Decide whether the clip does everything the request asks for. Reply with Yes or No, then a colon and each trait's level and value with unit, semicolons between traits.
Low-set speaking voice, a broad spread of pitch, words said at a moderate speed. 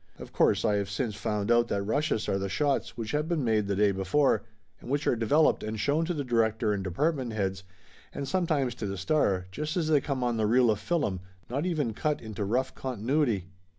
No: low, 120 Hz; wide, 5.8 semitones; fast, 220 wpm